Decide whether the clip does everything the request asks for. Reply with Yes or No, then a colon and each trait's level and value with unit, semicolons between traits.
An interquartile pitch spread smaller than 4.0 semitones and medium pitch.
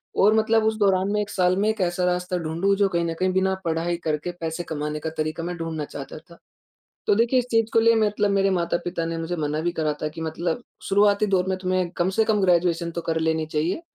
Yes: average, 3.5 semitones; medium, 180 Hz